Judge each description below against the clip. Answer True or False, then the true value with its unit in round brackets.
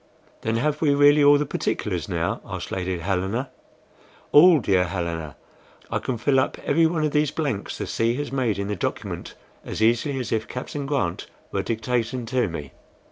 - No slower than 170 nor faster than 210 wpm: True (185 wpm)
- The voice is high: False (120 Hz)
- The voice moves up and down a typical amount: False (6.4 semitones)